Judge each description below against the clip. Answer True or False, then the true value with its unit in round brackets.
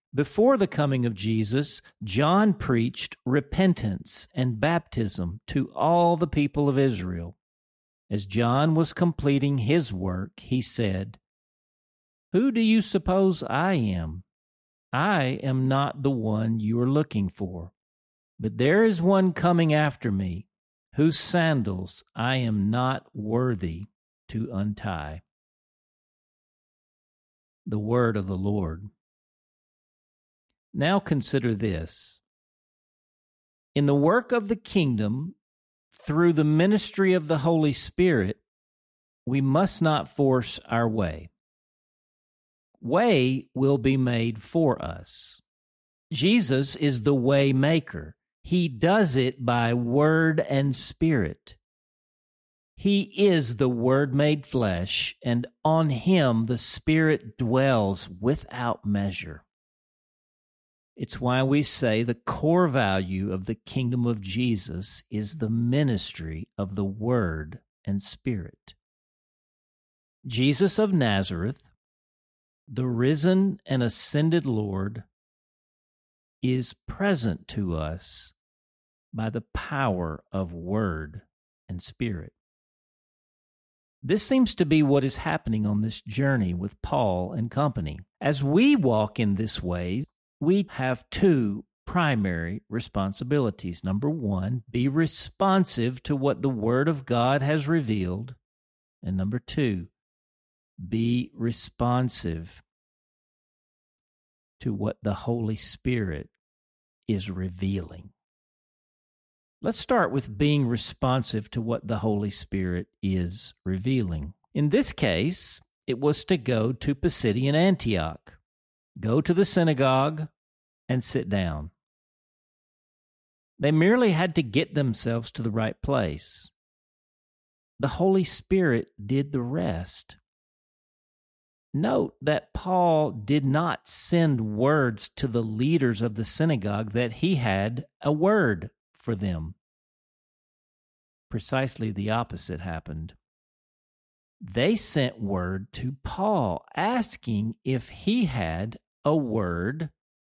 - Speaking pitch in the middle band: False (120 Hz)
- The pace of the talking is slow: True (110 wpm)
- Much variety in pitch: True (7.0 semitones)